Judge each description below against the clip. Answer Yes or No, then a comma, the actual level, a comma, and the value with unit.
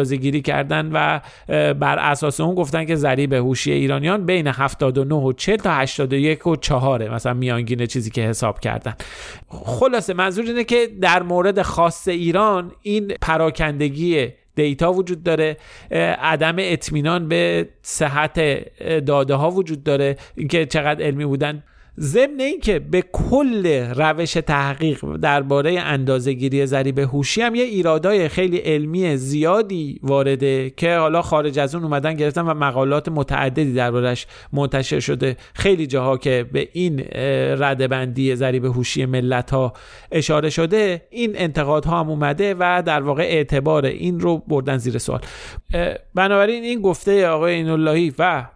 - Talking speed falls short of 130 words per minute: No, average, 140 wpm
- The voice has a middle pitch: Yes, medium, 150 Hz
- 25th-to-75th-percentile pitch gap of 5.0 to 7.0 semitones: No, average, 4.1 semitones